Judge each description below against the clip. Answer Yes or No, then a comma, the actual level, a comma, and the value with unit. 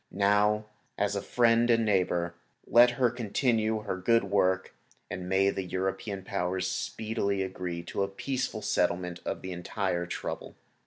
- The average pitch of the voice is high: No, low, 100 Hz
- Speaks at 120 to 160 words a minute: Yes, average, 150 wpm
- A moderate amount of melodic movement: Yes, average, 3.1 semitones